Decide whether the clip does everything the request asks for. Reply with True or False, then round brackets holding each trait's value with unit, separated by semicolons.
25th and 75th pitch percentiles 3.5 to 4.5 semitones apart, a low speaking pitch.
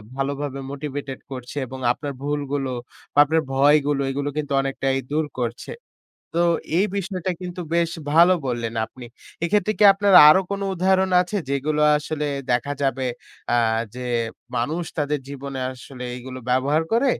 False (4.2 semitones; 145 Hz)